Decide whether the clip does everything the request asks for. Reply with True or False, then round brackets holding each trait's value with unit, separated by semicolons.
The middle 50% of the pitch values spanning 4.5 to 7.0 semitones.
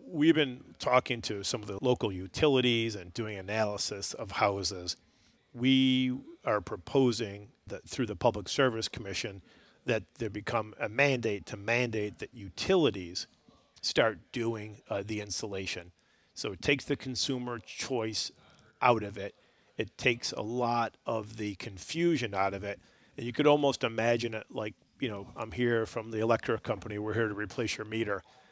False (3.5 semitones)